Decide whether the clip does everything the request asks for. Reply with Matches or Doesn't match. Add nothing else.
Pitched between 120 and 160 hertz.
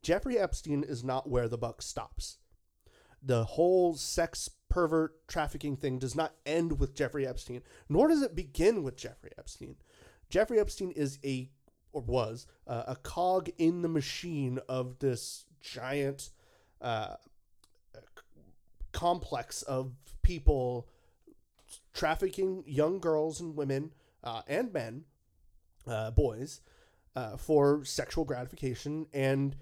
Matches